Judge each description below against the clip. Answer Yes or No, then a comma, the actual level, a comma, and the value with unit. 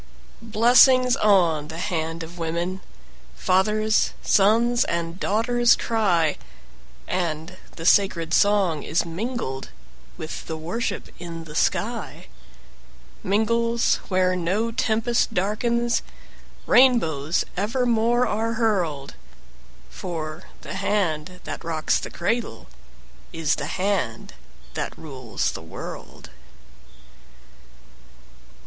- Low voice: No, medium, 185 Hz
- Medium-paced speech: No, slow, 95 wpm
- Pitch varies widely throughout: Yes, wide, 5.7 semitones